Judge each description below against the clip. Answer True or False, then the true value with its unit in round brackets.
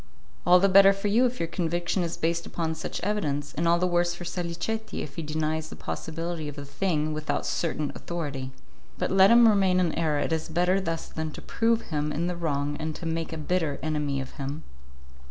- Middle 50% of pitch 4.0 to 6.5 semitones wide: False (2.9 semitones)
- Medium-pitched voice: True (165 Hz)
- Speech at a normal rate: False (215 wpm)